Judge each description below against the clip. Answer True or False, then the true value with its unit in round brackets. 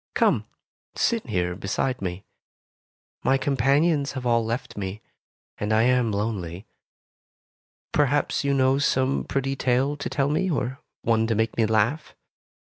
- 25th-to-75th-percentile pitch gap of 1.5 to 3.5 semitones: False (4.0 semitones)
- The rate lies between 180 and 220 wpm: False (140 wpm)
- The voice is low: True (125 Hz)